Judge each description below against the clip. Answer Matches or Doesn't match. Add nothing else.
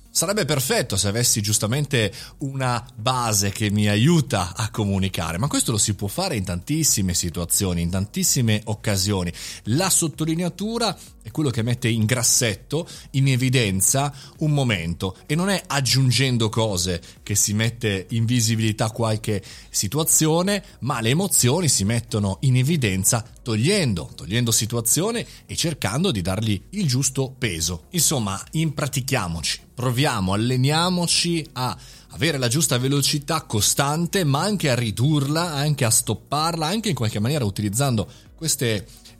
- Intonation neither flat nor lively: Doesn't match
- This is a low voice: Matches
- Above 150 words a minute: Doesn't match